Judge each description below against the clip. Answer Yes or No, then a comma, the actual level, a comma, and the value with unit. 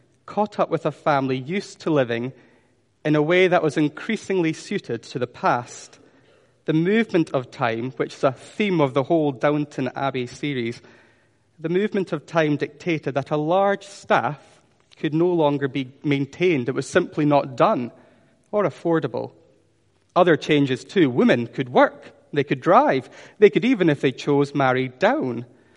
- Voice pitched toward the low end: No, medium, 150 Hz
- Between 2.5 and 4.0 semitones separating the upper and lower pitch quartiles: No, average, 4.8 semitones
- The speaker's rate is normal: Yes, average, 165 wpm